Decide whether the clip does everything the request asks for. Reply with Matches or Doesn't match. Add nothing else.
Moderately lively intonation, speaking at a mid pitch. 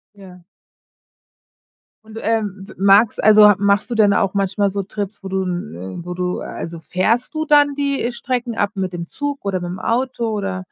Doesn't match